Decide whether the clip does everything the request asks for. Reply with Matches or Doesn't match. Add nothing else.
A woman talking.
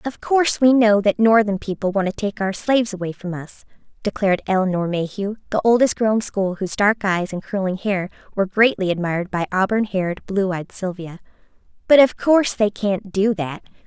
Matches